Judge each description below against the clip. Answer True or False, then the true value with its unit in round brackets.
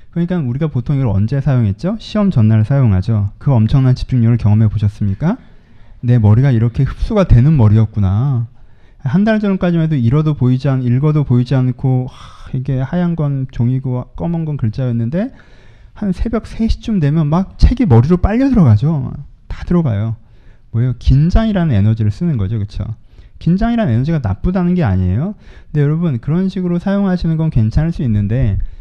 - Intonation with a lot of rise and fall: True (6.6 semitones)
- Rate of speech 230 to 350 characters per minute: False (380 characters per minute)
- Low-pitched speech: True (130 Hz)